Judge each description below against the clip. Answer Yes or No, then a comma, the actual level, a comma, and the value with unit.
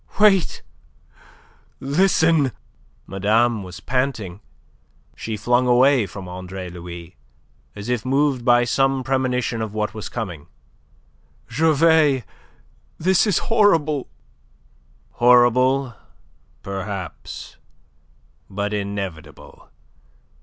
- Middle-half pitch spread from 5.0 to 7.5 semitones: Yes, wide, 5.6 semitones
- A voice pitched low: Yes, low, 120 Hz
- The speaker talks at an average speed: No, slow, 85 wpm